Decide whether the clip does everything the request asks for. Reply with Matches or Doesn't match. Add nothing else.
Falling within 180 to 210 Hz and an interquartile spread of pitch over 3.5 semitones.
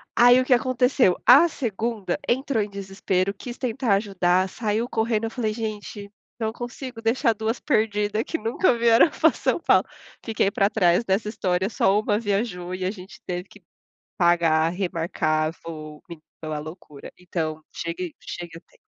Matches